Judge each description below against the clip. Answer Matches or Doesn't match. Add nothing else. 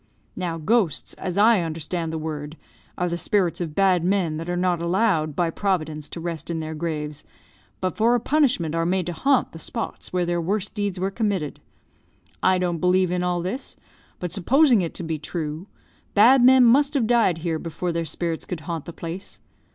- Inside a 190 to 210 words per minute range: Matches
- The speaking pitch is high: Doesn't match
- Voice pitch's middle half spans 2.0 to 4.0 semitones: Matches